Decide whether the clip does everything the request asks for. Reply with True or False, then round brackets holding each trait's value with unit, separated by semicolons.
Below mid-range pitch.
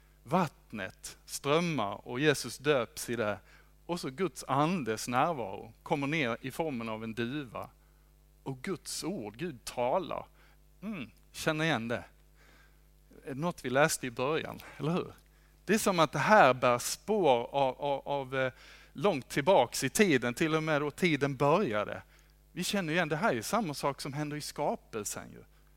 False (145 Hz)